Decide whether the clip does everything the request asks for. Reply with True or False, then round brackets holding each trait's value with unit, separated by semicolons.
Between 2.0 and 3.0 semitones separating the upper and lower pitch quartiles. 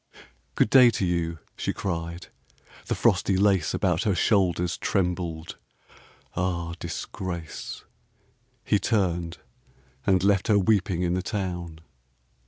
True (2.5 semitones)